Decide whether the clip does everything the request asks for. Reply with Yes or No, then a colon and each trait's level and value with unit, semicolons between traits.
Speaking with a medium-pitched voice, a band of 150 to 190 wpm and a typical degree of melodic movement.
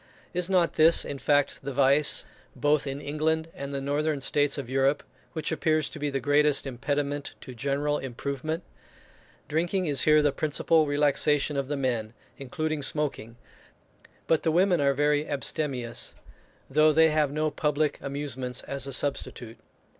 No: medium, 145 Hz; average, 155 wpm; narrow, 1.9 semitones